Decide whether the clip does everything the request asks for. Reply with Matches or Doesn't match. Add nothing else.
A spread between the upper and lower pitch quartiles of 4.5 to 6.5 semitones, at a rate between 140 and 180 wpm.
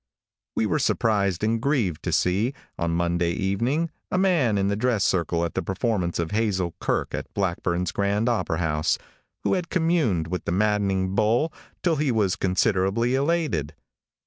Matches